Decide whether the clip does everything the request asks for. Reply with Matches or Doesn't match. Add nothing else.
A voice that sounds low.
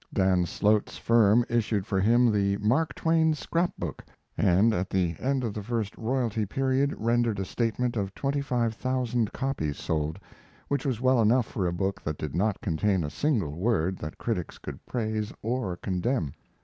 Matches